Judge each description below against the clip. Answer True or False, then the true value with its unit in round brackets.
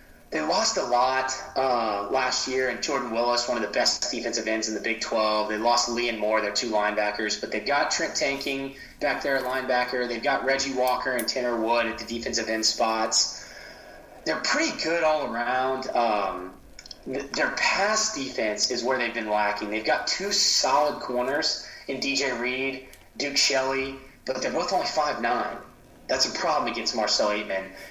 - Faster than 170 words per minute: True (180 wpm)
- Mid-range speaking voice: False (125 Hz)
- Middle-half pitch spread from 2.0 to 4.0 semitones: True (3.1 semitones)